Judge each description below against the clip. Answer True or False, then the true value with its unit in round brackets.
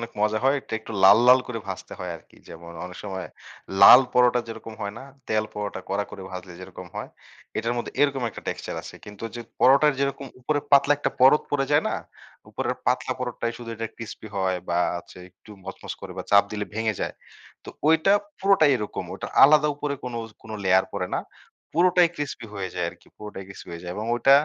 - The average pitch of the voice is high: False (115 Hz)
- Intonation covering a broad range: True (5.8 semitones)